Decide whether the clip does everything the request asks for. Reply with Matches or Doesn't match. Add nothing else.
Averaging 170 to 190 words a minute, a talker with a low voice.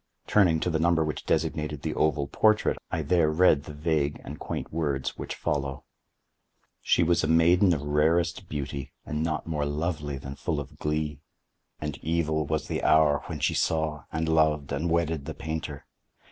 Matches